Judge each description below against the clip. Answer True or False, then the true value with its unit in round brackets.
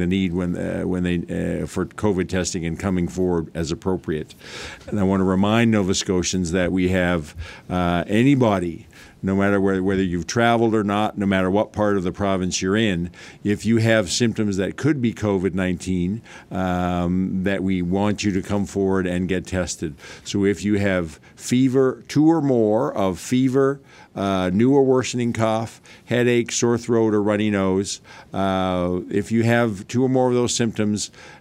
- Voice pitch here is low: True (100 Hz)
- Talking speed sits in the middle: True (180 wpm)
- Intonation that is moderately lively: True (3.5 semitones)